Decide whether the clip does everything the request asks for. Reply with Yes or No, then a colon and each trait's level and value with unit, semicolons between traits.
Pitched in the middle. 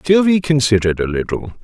No: low, 130 Hz